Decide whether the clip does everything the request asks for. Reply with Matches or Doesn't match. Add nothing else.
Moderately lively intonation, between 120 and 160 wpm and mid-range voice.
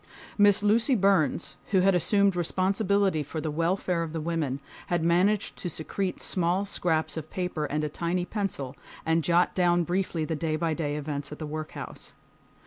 Doesn't match